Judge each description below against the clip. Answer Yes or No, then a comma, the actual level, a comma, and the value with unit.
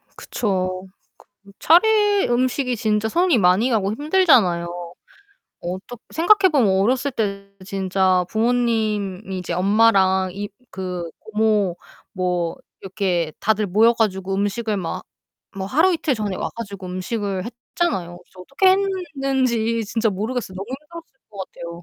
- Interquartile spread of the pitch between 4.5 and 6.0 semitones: Yes, average, 5.1 semitones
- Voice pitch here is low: No, high, 210 Hz